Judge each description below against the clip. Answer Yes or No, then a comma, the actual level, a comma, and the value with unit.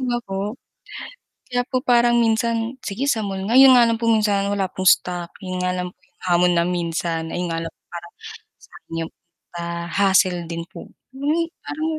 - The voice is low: No, high, 195 Hz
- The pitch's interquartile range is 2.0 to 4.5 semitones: No, average, 5.3 semitones